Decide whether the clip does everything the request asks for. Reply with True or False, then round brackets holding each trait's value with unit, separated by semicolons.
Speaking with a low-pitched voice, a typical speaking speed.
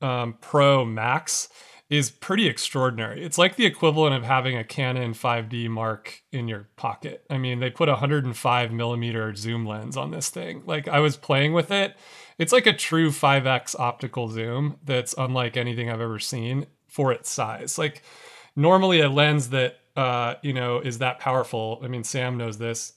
True (130 Hz; 180 wpm)